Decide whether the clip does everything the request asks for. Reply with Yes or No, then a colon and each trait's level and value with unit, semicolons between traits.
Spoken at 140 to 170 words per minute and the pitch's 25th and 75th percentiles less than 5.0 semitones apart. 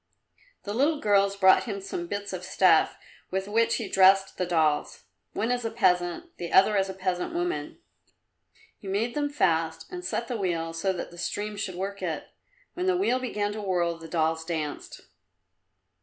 No: average, 185 wpm; average, 4.1 semitones